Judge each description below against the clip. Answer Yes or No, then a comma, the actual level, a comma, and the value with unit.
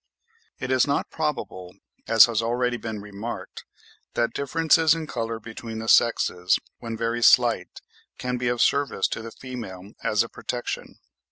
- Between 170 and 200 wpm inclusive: No, average, 155 wpm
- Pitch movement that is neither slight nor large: No, narrow, 2.2 semitones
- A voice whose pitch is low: Yes, low, 115 Hz